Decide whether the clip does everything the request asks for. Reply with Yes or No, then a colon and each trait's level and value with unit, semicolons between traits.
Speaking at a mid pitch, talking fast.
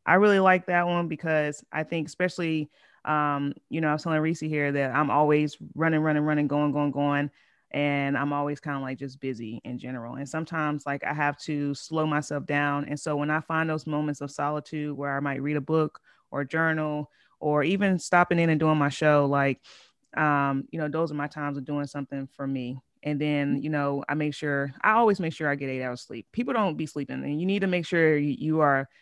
Yes: medium, 150 Hz; fast, 230 wpm